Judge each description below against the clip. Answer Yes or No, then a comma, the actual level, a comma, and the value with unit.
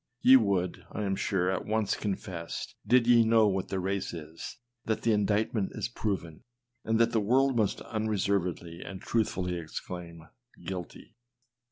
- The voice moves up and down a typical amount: Yes, average, 3.6 semitones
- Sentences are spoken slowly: No, average, 160 wpm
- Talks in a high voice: No, low, 100 Hz